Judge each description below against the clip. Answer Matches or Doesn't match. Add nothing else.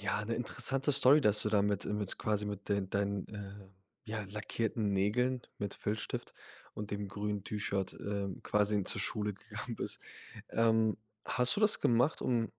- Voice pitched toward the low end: Matches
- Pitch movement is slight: Matches